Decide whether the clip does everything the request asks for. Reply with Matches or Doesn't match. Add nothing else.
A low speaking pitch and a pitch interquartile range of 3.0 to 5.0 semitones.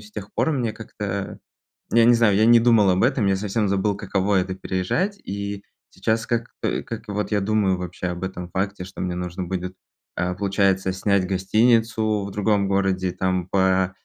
Doesn't match